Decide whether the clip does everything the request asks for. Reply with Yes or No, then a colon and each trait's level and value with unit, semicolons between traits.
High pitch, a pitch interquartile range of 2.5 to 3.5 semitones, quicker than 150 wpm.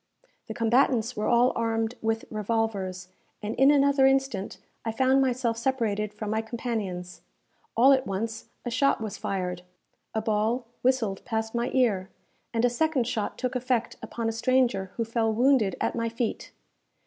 Yes: high, 230 Hz; average, 2.8 semitones; average, 160 wpm